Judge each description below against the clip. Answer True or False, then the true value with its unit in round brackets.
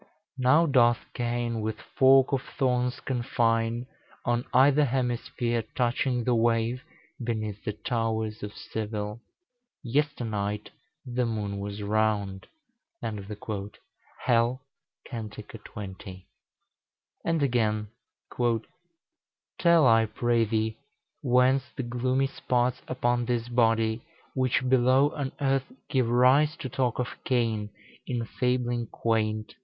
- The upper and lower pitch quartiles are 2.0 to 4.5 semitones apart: True (2.6 semitones)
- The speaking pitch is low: True (120 Hz)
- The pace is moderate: False (110 wpm)